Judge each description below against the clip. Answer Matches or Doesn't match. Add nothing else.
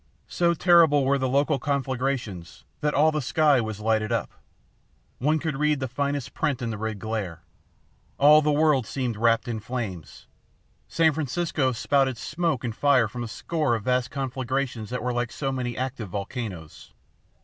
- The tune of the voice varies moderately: Matches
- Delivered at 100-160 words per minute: Doesn't match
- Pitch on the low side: Matches